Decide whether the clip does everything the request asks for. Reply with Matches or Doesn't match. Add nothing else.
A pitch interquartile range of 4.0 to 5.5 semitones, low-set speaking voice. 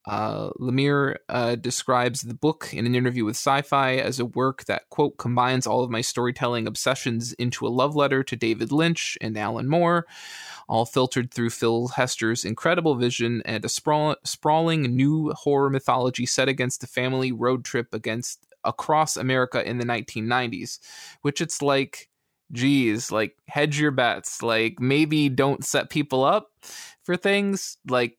Doesn't match